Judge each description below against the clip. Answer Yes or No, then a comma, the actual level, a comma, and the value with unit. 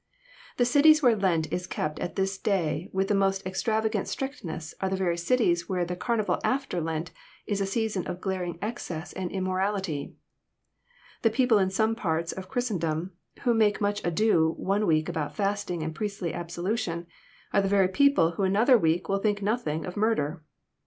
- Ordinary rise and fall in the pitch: Yes, average, 3.9 semitones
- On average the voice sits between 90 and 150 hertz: No, high, 190 Hz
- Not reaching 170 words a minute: No, average, 180 wpm